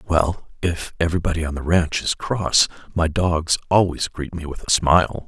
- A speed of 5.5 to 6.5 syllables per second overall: No, 4.8 syllables/s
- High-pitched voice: No, very low, 85 Hz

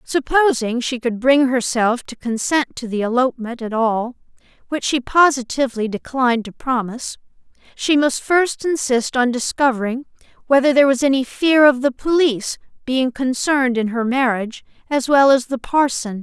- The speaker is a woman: Yes, female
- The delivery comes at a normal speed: Yes, average, 160 wpm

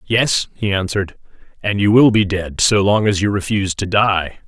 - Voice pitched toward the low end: Yes, low, 100 Hz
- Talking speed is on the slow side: No, average, 200 wpm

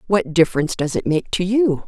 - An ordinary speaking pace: No, fast, 225 wpm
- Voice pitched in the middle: Yes, medium, 180 Hz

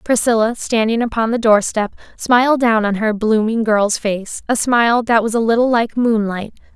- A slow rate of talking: No, average, 185 wpm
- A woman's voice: Yes, female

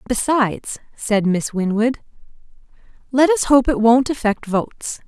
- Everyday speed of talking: No, slow, 130 wpm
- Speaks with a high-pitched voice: Yes, high, 235 Hz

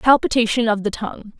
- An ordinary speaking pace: Yes, average, 170 wpm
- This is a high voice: Yes, high, 225 Hz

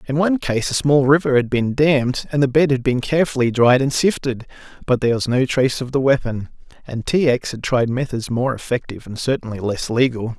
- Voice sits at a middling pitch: No, low, 130 Hz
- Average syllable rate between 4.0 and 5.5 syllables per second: No, 5.8 syllables/s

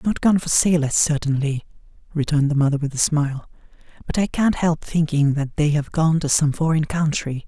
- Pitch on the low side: No, medium, 150 Hz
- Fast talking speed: No, average, 195 wpm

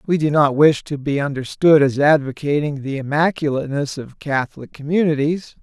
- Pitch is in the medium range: Yes, medium, 145 Hz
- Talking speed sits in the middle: Yes, average, 150 wpm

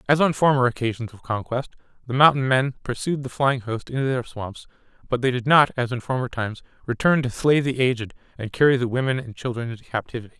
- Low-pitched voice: Yes, low, 125 Hz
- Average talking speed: No, fast, 215 wpm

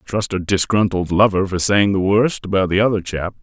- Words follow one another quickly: Yes, fast, 210 wpm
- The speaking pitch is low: Yes, very low, 95 Hz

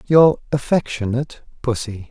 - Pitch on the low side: Yes, low, 130 Hz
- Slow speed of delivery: Yes, slow, 85 wpm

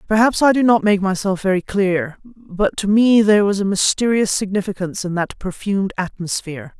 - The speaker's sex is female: Yes, female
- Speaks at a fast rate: No, average, 175 wpm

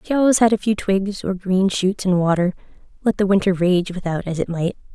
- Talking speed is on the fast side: Yes, fast, 220 wpm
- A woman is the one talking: Yes, female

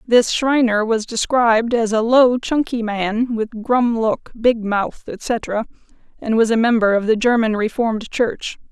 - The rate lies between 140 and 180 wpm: Yes, average, 165 wpm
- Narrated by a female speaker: Yes, female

